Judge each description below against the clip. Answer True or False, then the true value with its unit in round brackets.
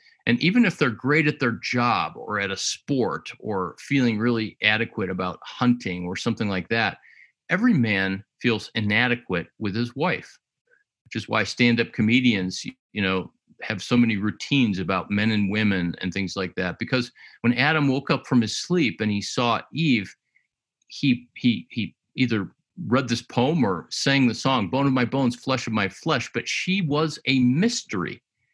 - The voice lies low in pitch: True (120 Hz)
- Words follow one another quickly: False (175 wpm)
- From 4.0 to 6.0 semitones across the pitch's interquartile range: True (4.3 semitones)